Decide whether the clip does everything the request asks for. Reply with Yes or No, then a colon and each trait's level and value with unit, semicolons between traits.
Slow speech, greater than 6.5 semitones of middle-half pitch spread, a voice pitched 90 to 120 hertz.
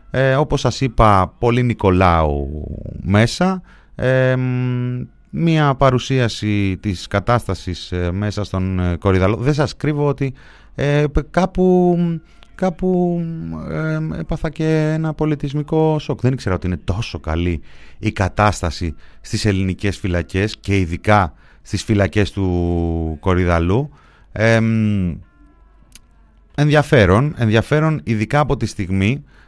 Yes: slow, 110 wpm; wide, 8.0 semitones; low, 110 Hz